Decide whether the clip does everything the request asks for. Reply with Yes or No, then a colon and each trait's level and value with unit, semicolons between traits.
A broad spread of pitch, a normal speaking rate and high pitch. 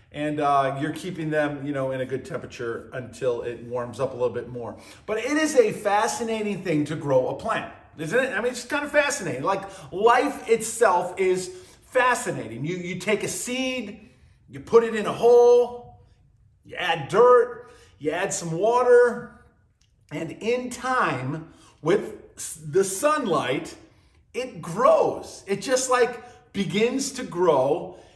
Yes: wide, 8.4 semitones; average, 160 wpm; high, 195 Hz